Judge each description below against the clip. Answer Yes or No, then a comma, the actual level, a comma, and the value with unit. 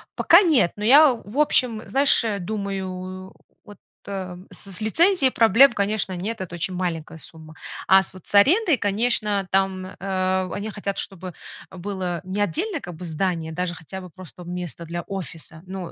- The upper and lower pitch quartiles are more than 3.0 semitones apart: Yes, average, 3.4 semitones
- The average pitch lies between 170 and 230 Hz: Yes, high, 190 Hz